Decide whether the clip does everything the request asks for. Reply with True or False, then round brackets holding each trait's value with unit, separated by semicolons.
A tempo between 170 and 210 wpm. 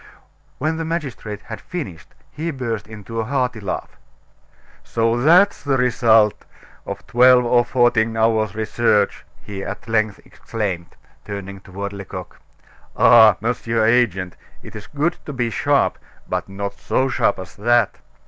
False (140 wpm)